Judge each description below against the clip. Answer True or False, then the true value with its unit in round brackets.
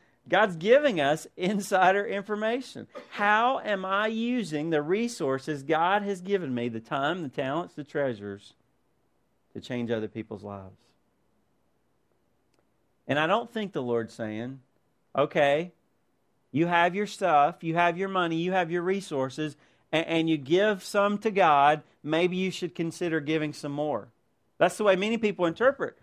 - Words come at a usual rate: True (150 wpm)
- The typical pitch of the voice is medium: True (165 Hz)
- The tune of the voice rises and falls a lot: True (5.9 semitones)